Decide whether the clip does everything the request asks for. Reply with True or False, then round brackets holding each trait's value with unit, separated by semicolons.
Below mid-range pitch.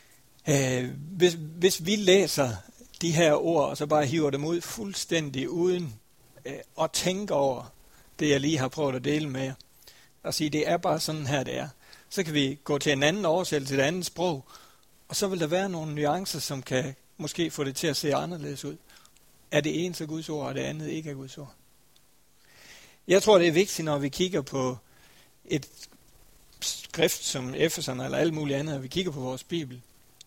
False (150 Hz)